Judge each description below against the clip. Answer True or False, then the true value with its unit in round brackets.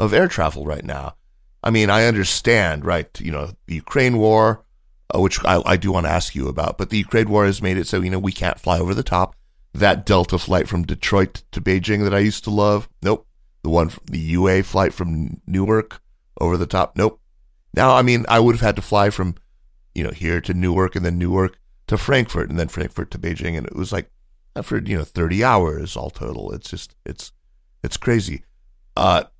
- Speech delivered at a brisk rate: True (220 wpm)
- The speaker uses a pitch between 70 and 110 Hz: True (95 Hz)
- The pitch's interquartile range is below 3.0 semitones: False (3.3 semitones)